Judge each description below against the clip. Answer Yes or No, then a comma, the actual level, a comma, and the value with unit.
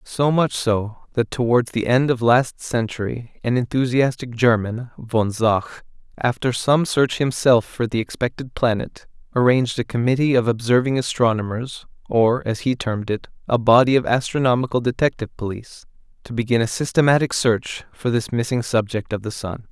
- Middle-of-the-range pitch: No, low, 120 Hz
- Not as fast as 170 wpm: Yes, average, 160 wpm